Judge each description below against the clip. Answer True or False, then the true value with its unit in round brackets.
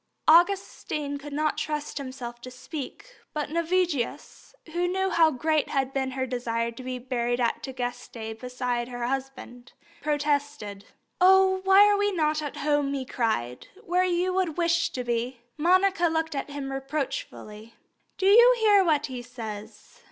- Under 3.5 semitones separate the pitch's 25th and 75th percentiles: False (5.5 semitones)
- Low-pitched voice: False (285 Hz)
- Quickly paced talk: False (155 wpm)